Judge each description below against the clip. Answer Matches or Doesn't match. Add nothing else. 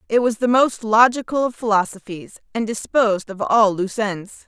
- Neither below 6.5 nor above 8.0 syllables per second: Doesn't match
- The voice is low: Doesn't match